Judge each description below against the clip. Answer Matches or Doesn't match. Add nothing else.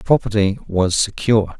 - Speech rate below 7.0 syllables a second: Matches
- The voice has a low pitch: Matches